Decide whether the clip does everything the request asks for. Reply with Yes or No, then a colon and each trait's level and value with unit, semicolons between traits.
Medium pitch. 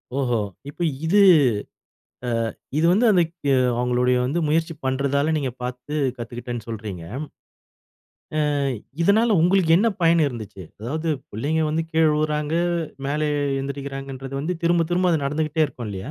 Yes: medium, 145 Hz